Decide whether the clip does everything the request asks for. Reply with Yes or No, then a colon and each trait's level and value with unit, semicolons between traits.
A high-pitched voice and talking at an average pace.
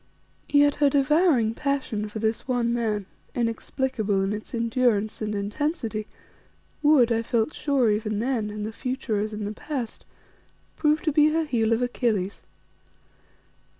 Yes: high, 230 Hz; average, 150 wpm